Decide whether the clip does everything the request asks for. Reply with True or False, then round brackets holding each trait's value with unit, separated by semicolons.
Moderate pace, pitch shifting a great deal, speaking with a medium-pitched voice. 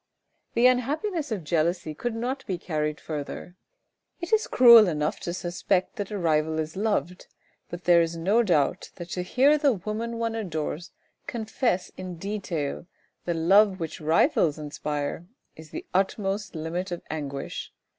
True (155 wpm; 5.7 semitones; 180 Hz)